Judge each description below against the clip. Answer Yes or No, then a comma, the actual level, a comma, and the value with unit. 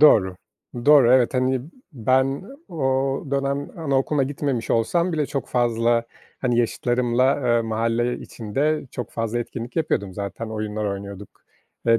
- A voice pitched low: Yes, low, 120 Hz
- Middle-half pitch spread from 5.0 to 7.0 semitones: No, average, 3.2 semitones